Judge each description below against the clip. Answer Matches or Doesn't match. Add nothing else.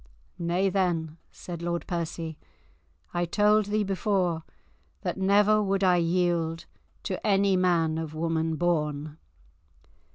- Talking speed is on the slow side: Matches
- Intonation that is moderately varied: Matches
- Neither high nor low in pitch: Matches